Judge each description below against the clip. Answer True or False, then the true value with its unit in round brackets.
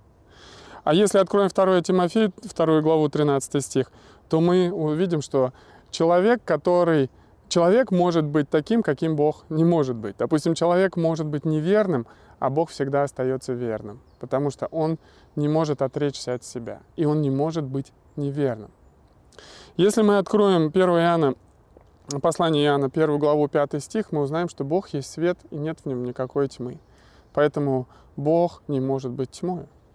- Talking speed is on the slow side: False (155 wpm)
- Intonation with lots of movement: False (4.0 semitones)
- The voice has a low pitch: False (150 Hz)